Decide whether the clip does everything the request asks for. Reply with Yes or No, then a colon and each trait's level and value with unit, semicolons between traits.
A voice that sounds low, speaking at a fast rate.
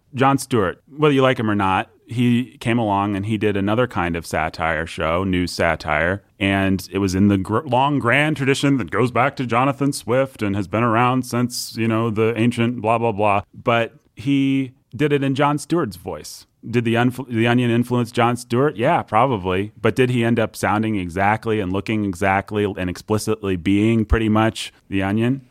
No: low, 115 Hz; average, 195 wpm